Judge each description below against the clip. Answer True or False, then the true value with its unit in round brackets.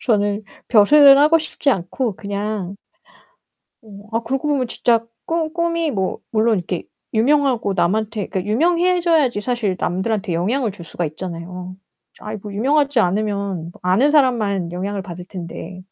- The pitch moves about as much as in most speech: False (6.2 semitones)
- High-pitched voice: True (215 Hz)